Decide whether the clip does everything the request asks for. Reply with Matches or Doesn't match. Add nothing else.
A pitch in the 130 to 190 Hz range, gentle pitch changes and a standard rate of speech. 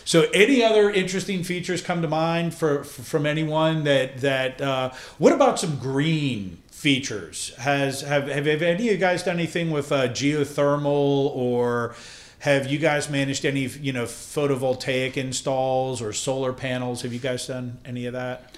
Doesn't match